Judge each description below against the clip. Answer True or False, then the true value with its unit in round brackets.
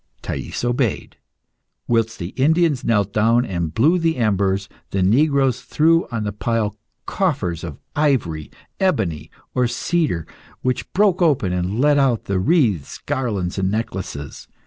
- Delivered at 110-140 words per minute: True (135 wpm)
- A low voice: True (115 Hz)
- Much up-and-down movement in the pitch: True (6.9 semitones)